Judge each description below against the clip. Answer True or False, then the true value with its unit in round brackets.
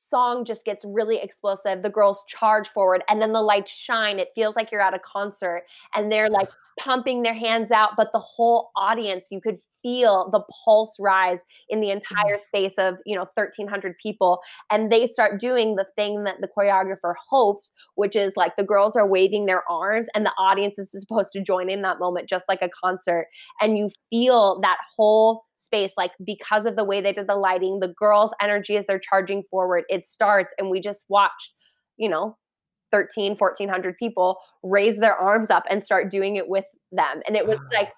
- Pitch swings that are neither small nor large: False (2.1 semitones)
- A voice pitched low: False (205 Hz)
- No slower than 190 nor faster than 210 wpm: True (200 wpm)